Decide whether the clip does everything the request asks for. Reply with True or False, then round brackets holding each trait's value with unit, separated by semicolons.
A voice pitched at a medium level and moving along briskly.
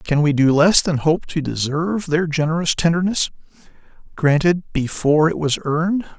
False (160 Hz; 155 wpm)